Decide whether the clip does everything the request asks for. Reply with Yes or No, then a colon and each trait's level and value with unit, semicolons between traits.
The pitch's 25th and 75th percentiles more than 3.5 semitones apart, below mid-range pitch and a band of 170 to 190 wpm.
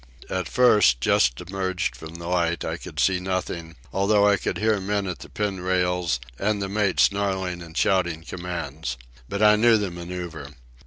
No: average, 2.9 semitones; very low, 90 Hz; average, 175 wpm